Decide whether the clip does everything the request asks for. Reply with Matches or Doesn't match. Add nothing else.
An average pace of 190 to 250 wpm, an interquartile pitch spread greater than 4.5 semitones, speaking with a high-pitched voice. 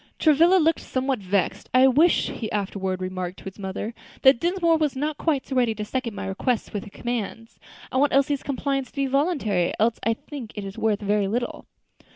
Matches